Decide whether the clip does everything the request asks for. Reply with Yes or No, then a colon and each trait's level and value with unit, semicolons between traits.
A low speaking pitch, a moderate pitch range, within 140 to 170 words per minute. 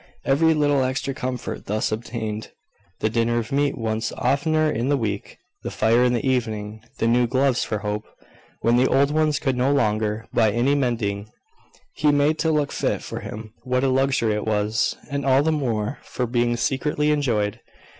No: low, 125 Hz; average, 4.2 semitones; average, 185 wpm